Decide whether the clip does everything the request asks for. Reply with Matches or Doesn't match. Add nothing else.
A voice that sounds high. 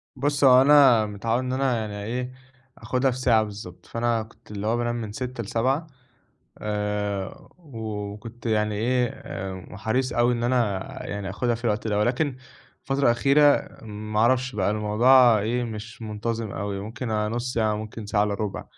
Doesn't match